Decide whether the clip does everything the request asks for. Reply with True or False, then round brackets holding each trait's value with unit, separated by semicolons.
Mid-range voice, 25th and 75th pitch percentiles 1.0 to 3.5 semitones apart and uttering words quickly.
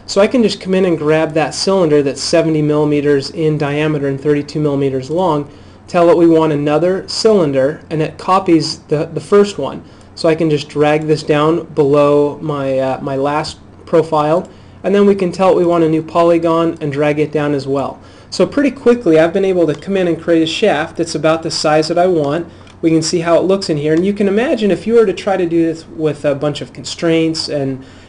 True (160 Hz; 2.8 semitones; 230 wpm)